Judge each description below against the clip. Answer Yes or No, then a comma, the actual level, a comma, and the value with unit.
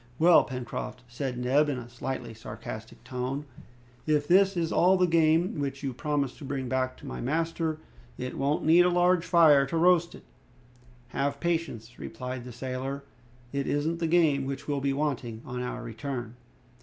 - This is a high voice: No, medium, 140 Hz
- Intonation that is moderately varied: Yes, average, 4.4 semitones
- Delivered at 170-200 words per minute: Yes, average, 175 wpm